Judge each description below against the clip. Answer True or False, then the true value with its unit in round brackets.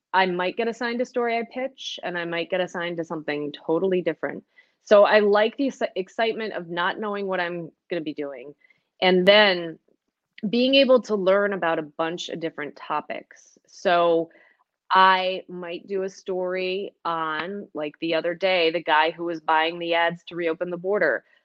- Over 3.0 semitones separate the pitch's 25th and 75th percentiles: True (3.4 semitones)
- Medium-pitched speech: True (180 Hz)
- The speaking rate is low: False (180 wpm)